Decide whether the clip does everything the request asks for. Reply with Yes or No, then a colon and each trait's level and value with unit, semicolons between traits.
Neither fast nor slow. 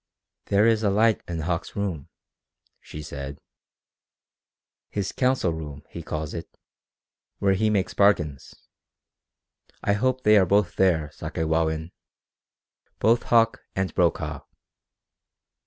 No: slow, 115 wpm